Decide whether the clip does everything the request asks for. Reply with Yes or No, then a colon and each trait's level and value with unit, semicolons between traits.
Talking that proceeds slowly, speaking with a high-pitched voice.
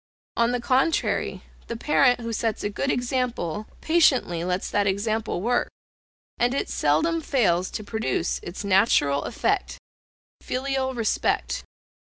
Yes: slow, 130 wpm; high, 235 Hz